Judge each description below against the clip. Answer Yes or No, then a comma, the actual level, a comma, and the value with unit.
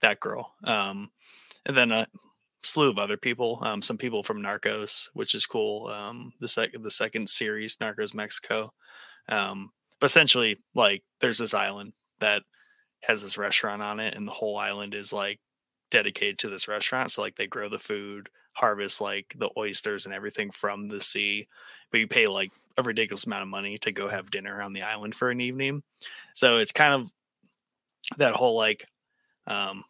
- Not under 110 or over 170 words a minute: No, average, 185 wpm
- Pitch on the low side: Yes, low, 105 Hz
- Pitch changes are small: No, average, 3.0 semitones